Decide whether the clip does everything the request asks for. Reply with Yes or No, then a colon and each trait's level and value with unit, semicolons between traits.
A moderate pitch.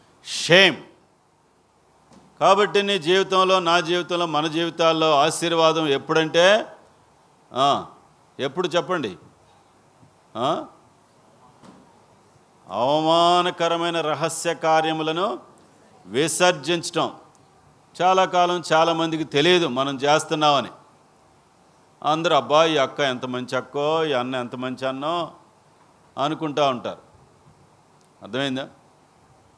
Yes: medium, 160 Hz